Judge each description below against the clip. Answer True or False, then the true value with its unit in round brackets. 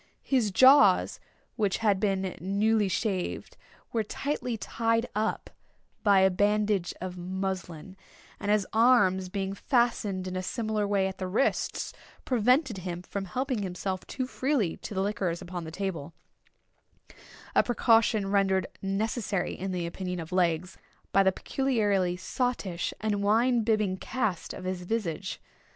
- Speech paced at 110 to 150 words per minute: True (140 wpm)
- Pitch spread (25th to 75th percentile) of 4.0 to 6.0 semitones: False (3.2 semitones)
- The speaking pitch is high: True (195 Hz)